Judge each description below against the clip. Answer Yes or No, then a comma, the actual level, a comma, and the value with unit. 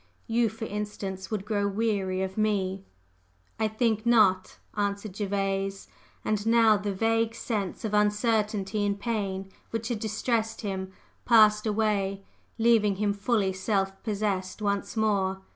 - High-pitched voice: Yes, high, 210 Hz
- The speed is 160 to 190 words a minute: No, slow, 135 wpm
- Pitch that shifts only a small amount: Yes, narrow, 2.1 semitones